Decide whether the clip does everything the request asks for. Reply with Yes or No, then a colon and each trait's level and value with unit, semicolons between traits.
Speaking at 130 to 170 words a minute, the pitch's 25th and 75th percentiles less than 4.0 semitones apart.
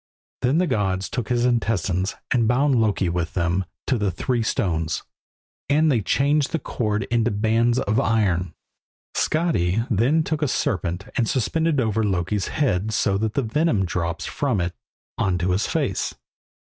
No: average, 165 wpm; wide, 5.4 semitones